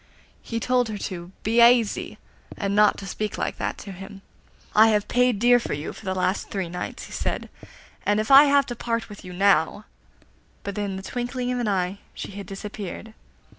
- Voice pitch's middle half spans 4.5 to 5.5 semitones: No, average, 3.5 semitones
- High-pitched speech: Yes, high, 210 Hz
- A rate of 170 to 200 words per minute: Yes, average, 195 wpm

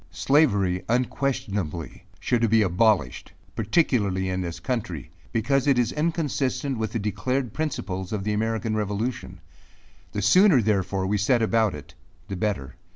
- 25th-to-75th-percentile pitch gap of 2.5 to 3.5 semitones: No, average, 4.7 semitones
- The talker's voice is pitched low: Yes, low, 110 Hz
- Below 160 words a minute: Yes, average, 140 wpm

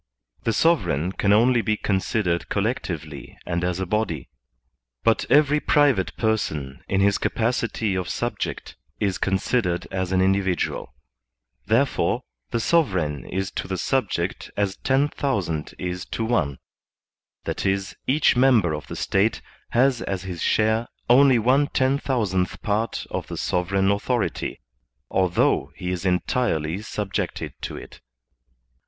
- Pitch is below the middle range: Yes, low, 100 Hz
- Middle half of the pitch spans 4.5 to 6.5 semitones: Yes, average, 4.8 semitones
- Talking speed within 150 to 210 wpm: No, slow, 135 wpm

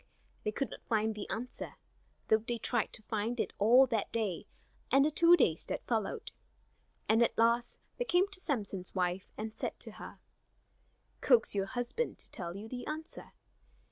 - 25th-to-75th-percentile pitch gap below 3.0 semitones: No, average, 4.1 semitones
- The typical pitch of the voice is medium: No, high, 230 Hz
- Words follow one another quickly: No, average, 175 wpm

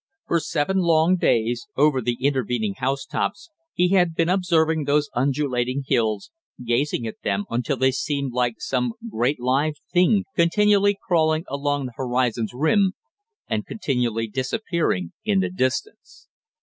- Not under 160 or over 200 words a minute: No, slow, 135 wpm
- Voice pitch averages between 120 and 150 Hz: Yes, medium, 140 Hz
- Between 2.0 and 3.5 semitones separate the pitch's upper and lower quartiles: No, wide, 5.5 semitones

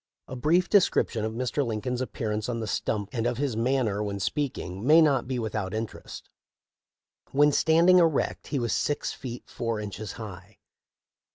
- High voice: No, low, 120 Hz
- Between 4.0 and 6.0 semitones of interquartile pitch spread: Yes, average, 4.8 semitones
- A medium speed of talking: Yes, average, 165 wpm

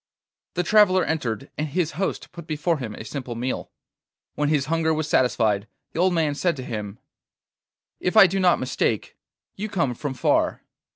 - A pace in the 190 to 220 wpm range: No, average, 175 wpm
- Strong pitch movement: Yes, wide, 5.7 semitones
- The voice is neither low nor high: Yes, medium, 150 Hz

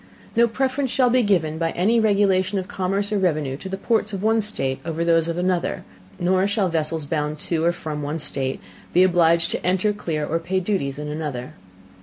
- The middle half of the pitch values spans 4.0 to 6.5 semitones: Yes, average, 4.3 semitones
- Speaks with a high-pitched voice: No, medium, 180 Hz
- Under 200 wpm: No, fast, 205 wpm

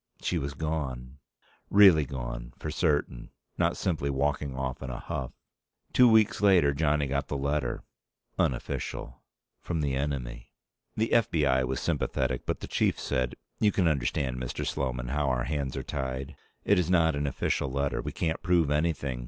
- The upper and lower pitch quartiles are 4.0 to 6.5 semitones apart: No, average, 3.5 semitones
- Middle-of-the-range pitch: No, very low, 70 Hz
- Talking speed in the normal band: Yes, average, 165 wpm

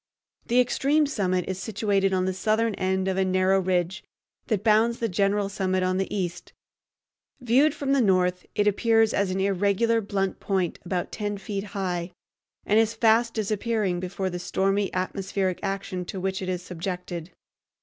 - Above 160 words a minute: Yes, average, 170 wpm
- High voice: Yes, high, 195 Hz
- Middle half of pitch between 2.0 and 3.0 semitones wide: Yes, narrow, 2.6 semitones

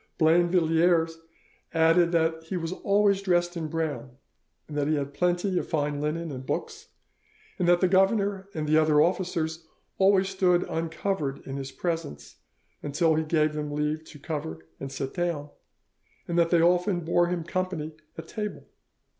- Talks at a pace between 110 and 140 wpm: No, average, 155 wpm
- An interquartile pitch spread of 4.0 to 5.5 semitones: No, average, 2.8 semitones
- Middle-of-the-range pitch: Yes, medium, 165 Hz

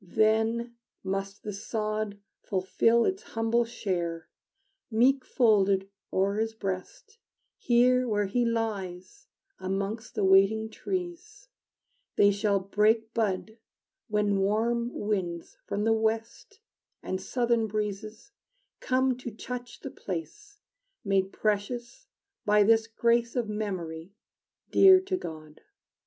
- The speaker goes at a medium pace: No, slow, 115 wpm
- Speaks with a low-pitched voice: No, high, 220 Hz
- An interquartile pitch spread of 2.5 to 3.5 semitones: Yes, average, 3.2 semitones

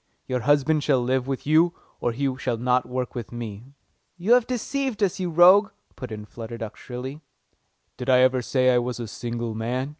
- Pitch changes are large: No, average, 4.4 semitones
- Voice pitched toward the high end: No, low, 130 Hz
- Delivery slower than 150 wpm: No, average, 200 wpm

